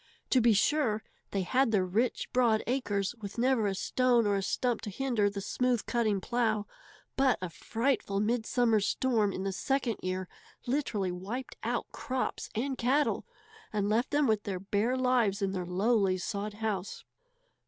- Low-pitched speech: No, high, 220 Hz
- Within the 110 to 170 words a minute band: Yes, average, 165 wpm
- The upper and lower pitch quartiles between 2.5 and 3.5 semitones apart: No, average, 4.0 semitones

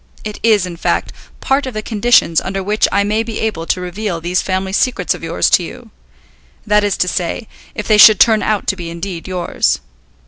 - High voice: Yes, high, 200 Hz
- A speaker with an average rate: No, fast, 210 wpm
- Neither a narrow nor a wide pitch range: Yes, average, 3.2 semitones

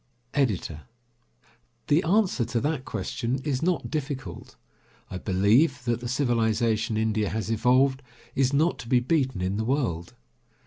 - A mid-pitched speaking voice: No, low, 125 Hz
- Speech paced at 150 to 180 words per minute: No, average, 140 wpm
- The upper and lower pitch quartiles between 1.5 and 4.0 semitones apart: No, average, 4.4 semitones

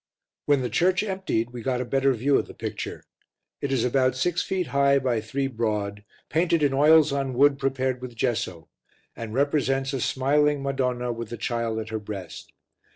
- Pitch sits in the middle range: No, low, 130 Hz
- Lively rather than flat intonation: No, average, 3.2 semitones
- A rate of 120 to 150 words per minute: No, average, 185 wpm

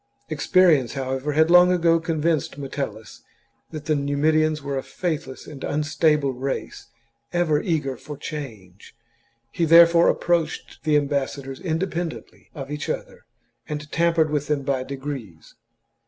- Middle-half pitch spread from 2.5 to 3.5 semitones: Yes, average, 3.1 semitones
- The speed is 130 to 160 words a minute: Yes, slow, 135 wpm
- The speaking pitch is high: No, medium, 150 Hz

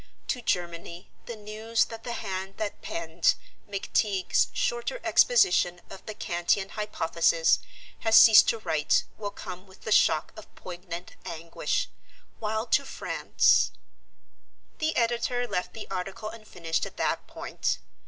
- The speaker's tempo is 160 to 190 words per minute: No, slow, 135 wpm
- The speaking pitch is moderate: No, high, 205 Hz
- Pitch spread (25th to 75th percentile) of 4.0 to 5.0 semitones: Yes, average, 4.4 semitones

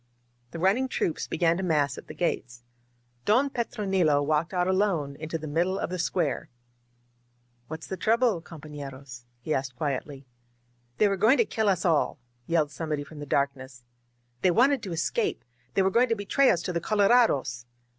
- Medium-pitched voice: Yes, medium, 170 Hz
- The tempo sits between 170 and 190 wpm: Yes, average, 185 wpm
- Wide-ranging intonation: Yes, wide, 5.7 semitones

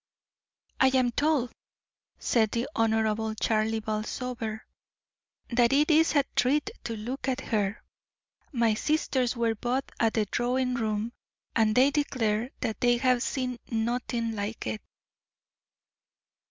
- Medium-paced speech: No, slow, 125 wpm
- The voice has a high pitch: Yes, high, 235 Hz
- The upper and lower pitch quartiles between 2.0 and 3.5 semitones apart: Yes, narrow, 2.6 semitones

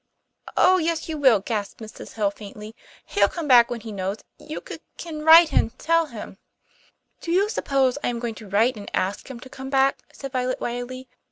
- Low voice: No, very high, 255 Hz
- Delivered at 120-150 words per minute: No, fast, 205 wpm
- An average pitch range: No, wide, 5.7 semitones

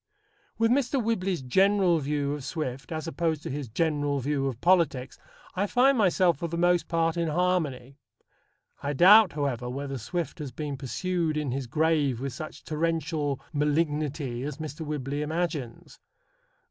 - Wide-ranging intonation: No, average, 3.7 semitones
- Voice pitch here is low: No, medium, 150 Hz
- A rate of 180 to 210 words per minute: No, average, 155 wpm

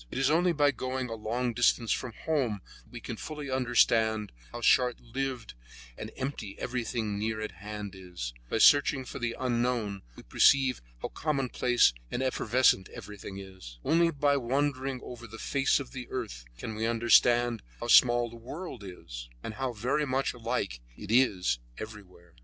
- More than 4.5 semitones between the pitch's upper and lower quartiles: No, average, 3.7 semitones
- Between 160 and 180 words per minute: Yes, average, 170 wpm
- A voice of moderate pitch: No, low, 120 Hz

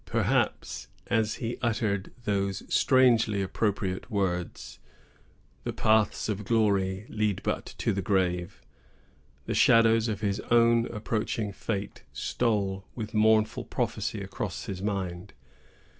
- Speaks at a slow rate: Yes, slow, 115 wpm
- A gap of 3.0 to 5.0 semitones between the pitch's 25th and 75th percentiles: No, narrow, 2.5 semitones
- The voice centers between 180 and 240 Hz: No, low, 105 Hz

